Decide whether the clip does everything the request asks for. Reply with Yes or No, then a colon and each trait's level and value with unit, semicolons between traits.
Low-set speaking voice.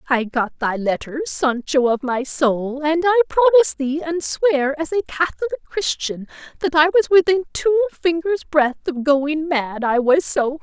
No: very high, 305 Hz